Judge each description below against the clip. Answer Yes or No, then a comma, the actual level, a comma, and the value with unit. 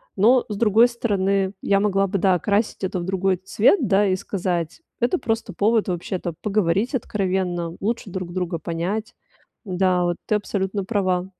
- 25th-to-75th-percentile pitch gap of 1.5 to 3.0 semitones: Yes, narrow, 2.6 semitones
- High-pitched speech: Yes, high, 195 Hz